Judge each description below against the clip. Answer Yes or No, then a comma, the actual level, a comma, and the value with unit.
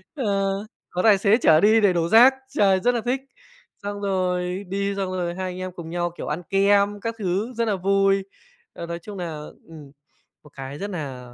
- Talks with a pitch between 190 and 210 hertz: Yes, high, 195 Hz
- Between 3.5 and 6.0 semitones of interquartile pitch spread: No, average, 2.7 semitones